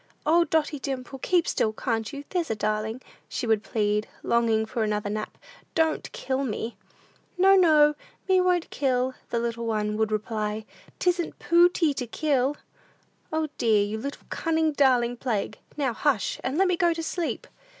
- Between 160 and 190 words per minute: Yes, average, 165 wpm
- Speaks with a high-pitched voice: Yes, very high, 260 Hz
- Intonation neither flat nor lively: No, wide, 6.4 semitones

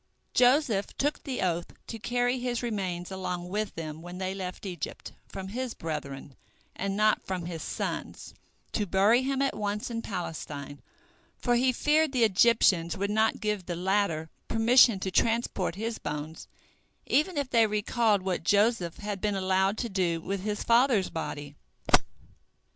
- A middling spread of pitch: Yes, average, 4.7 semitones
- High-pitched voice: Yes, high, 200 Hz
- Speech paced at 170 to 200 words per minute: No, average, 160 wpm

